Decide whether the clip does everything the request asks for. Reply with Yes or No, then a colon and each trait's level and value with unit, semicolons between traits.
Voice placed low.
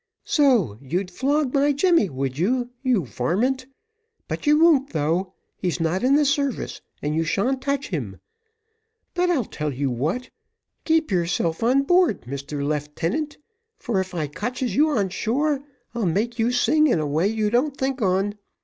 No: high, 225 Hz